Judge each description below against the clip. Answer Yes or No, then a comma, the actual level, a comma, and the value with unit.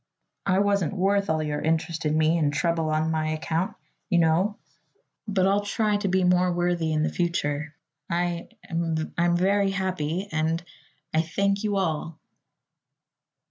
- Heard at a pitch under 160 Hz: No, medium, 175 Hz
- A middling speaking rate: Yes, average, 155 wpm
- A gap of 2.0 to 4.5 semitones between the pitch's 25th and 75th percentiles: Yes, average, 3.5 semitones